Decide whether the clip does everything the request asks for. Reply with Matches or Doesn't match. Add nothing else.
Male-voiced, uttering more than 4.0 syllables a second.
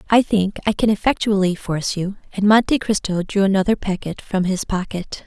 Doesn't match